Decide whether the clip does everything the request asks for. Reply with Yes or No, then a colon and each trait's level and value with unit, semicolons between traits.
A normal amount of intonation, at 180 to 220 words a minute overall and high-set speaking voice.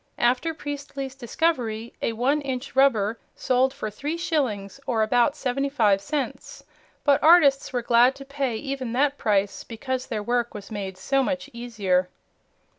No: average, 4.0 semitones; average, 155 wpm; very high, 255 Hz